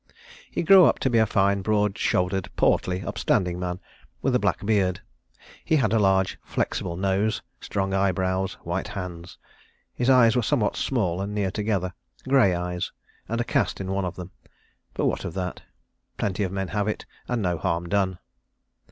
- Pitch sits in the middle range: No, very low, 95 Hz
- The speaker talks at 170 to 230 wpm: Yes, average, 175 wpm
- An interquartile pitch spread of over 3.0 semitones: No, average, 2.7 semitones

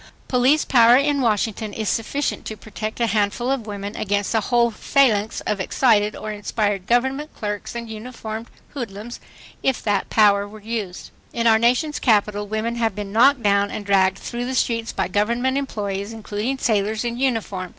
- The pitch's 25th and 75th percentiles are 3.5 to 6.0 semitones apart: No, average, 2.8 semitones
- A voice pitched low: No, high, 220 Hz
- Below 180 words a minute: Yes, average, 170 wpm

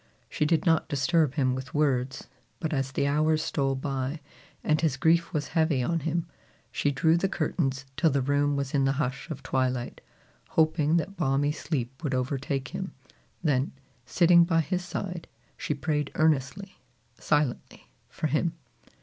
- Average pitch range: Yes, average, 3.2 semitones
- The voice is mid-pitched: Yes, medium, 145 Hz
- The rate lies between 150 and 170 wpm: Yes, average, 160 wpm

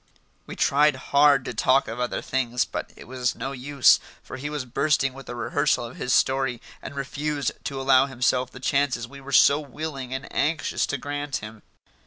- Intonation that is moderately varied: No, narrow, 2.2 semitones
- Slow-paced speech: No, average, 195 wpm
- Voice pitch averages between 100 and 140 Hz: Yes, low, 135 Hz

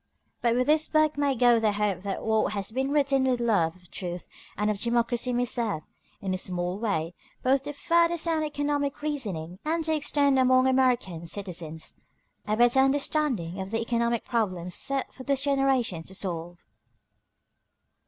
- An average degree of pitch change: No, wide, 6.3 semitones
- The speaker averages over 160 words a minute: Yes, average, 170 wpm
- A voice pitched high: Yes, high, 240 Hz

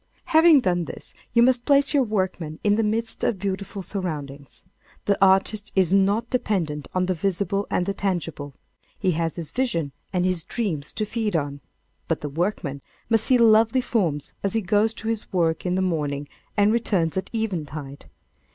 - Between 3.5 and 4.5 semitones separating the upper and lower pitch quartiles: No, average, 5.1 semitones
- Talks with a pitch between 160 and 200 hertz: Yes, high, 190 Hz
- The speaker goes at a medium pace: Yes, average, 180 wpm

